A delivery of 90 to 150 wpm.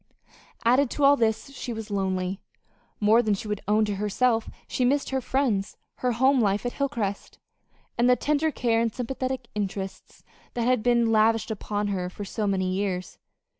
No: average, 175 wpm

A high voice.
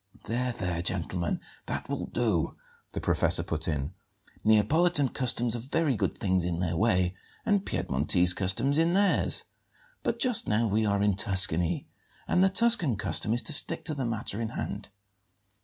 No: low, 110 Hz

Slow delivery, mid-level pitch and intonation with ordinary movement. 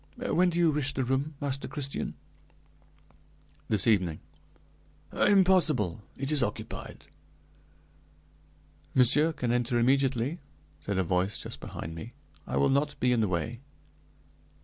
No: slow, 125 wpm; low, 130 Hz; average, 4.9 semitones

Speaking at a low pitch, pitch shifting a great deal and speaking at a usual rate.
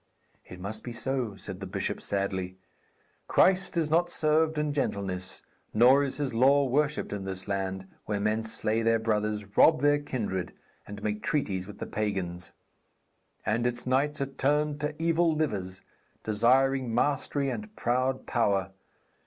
Yes: low, 115 Hz; wide, 6.4 semitones; average, 155 wpm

